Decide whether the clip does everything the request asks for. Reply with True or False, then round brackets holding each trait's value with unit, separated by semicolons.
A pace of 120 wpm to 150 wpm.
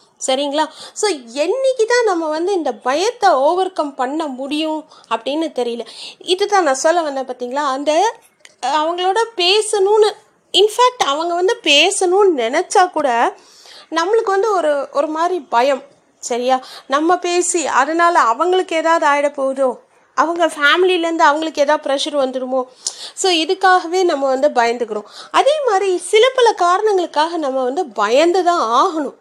True (130 wpm)